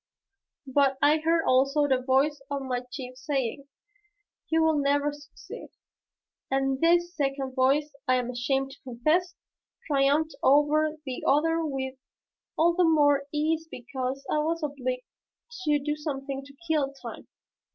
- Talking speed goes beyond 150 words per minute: No, average, 140 wpm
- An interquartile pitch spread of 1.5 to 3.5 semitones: Yes, narrow, 2.4 semitones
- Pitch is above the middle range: Yes, very high, 285 Hz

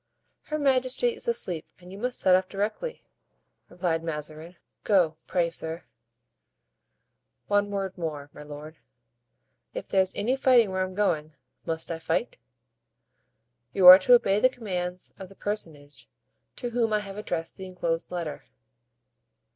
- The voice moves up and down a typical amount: Yes, average, 4.3 semitones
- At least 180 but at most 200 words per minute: No, average, 145 wpm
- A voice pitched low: No, medium, 185 Hz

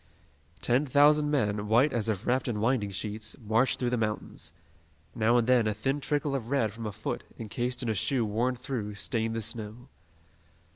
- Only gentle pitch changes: No, average, 3.2 semitones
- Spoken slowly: No, average, 190 wpm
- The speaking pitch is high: No, low, 115 Hz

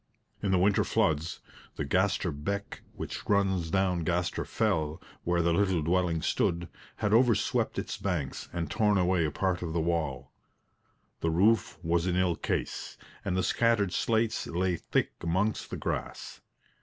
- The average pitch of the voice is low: Yes, very low, 90 Hz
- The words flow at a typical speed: Yes, average, 155 wpm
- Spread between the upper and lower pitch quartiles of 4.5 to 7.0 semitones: No, average, 3.1 semitones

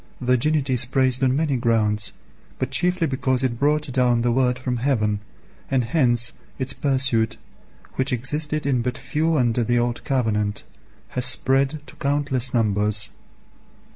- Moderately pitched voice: No, low, 130 Hz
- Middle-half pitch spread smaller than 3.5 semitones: Yes, narrow, 2.6 semitones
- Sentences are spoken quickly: No, average, 145 wpm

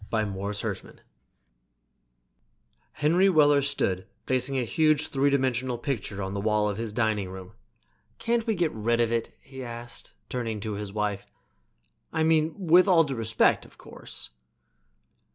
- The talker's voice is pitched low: Yes, low, 120 Hz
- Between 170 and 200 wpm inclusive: No, average, 150 wpm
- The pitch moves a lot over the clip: Yes, wide, 6.1 semitones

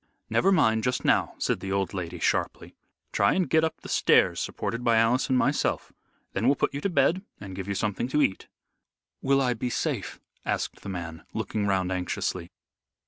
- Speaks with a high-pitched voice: No, low, 110 Hz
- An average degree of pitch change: No, wide, 6.1 semitones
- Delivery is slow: No, average, 195 wpm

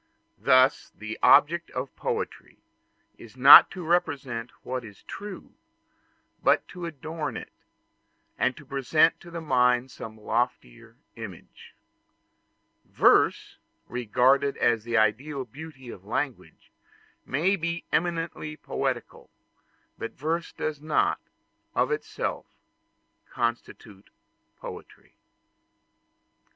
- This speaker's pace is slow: Yes, slow, 100 wpm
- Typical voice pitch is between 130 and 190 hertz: Yes, low, 135 Hz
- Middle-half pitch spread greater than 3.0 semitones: Yes, average, 5.1 semitones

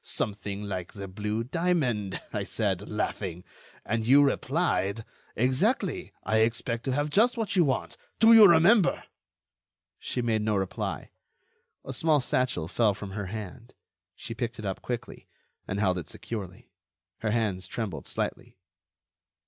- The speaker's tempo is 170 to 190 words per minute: No, average, 145 wpm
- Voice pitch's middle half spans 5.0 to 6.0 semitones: Yes, average, 5.3 semitones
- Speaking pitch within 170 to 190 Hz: No, low, 115 Hz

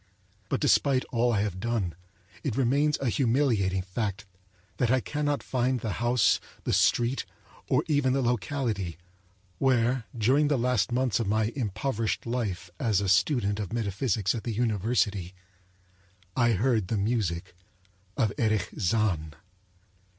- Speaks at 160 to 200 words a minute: No, average, 140 wpm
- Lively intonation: No, average, 4.1 semitones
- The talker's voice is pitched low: Yes, low, 115 Hz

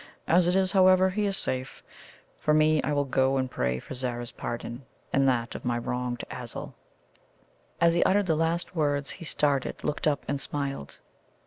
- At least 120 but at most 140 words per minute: No, average, 185 wpm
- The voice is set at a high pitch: No, medium, 145 Hz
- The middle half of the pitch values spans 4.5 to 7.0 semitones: Yes, average, 4.8 semitones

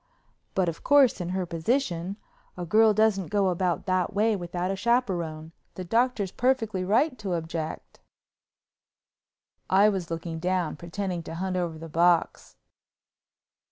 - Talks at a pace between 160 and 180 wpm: No, average, 140 wpm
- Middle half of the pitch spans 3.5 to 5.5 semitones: Yes, average, 3.8 semitones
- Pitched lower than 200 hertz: Yes, medium, 185 Hz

